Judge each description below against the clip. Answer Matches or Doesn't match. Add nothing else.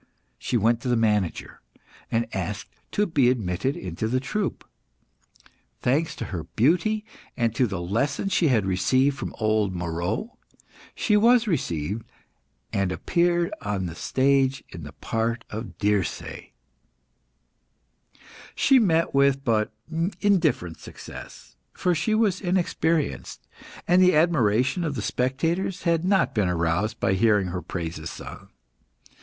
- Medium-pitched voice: Doesn't match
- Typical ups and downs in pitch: Doesn't match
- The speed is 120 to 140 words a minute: Matches